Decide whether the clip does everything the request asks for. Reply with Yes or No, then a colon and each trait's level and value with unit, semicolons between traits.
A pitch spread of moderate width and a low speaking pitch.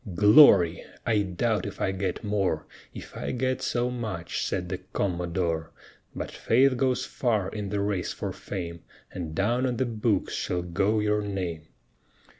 Yes: average, 4.3 semitones; low, 100 Hz